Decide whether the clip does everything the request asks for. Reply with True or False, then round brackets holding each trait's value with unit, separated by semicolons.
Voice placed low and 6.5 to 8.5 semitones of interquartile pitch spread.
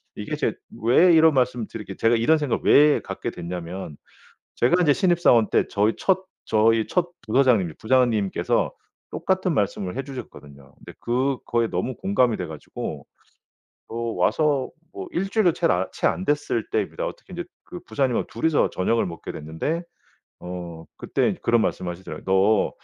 True (120 Hz; 7.8 semitones)